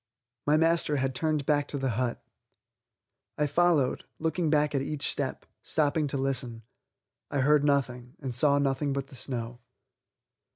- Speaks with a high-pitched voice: No, medium, 140 Hz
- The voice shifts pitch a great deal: No, narrow, 2.4 semitones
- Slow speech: No, average, 155 wpm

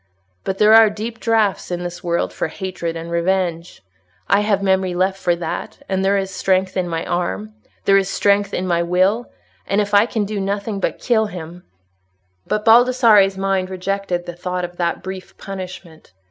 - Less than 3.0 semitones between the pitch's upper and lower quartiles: Yes, narrow, 2.5 semitones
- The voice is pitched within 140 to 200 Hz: Yes, high, 190 Hz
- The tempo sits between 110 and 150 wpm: No, average, 175 wpm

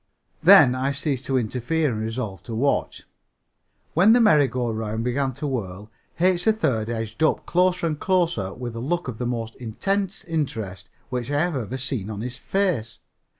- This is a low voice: Yes, low, 130 Hz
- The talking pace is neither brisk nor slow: Yes, average, 180 wpm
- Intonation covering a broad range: Yes, wide, 6.3 semitones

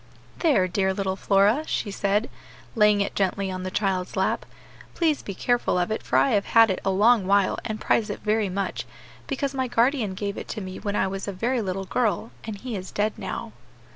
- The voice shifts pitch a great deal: No, average, 3.0 semitones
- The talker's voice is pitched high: Yes, high, 205 Hz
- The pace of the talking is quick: Yes, fast, 215 wpm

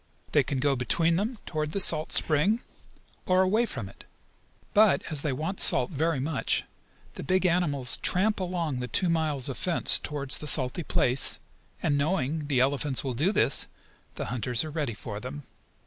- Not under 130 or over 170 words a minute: No, average, 180 wpm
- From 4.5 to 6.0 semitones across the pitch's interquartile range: Yes, average, 5.0 semitones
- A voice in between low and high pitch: Yes, medium, 150 Hz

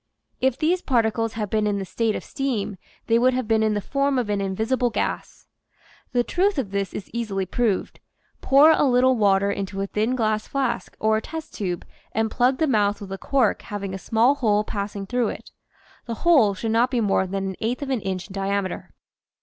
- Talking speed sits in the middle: No, fast, 215 wpm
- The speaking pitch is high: Yes, high, 220 Hz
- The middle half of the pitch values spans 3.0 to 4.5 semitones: Yes, average, 4.1 semitones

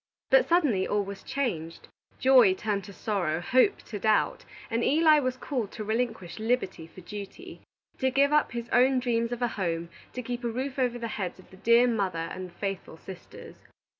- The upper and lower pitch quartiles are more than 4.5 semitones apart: Yes, average, 5.0 semitones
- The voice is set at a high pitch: Yes, high, 230 Hz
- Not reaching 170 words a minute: No, average, 195 wpm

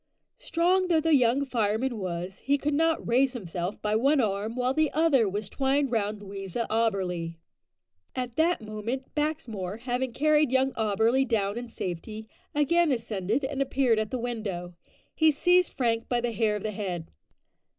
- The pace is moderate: Yes, average, 165 wpm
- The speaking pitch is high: Yes, high, 235 Hz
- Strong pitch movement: No, average, 4.8 semitones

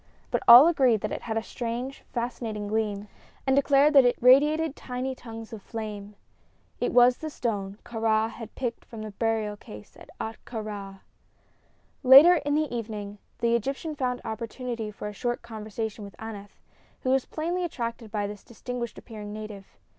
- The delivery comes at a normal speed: Yes, average, 170 wpm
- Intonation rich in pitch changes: No, average, 3.2 semitones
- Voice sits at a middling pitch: No, high, 230 Hz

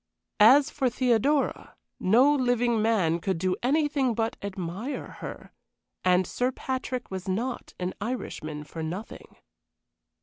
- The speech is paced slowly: Yes, slow, 125 wpm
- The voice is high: Yes, high, 225 Hz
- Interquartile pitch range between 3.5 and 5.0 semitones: No, wide, 5.6 semitones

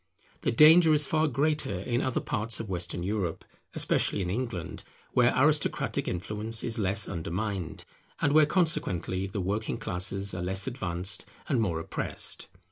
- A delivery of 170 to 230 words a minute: No, average, 150 wpm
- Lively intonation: Yes, wide, 6.0 semitones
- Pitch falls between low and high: No, low, 105 Hz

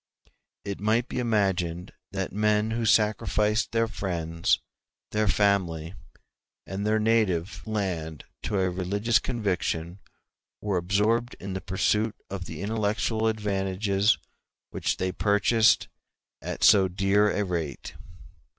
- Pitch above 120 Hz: No, low, 100 Hz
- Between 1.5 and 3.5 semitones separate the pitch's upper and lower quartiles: Yes, average, 2.8 semitones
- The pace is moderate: No, slow, 120 wpm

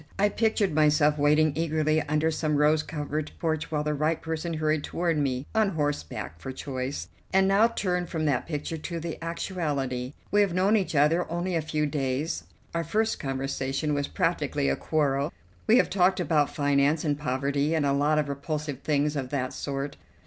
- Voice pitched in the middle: Yes, medium, 150 Hz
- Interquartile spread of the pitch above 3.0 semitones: No, narrow, 2.6 semitones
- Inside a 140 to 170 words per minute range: No, average, 185 wpm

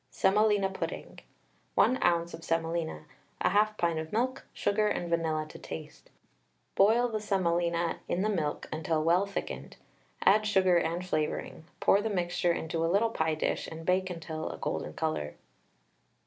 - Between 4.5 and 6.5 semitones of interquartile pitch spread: No, average, 3.7 semitones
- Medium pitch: Yes, medium, 175 Hz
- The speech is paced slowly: No, average, 155 wpm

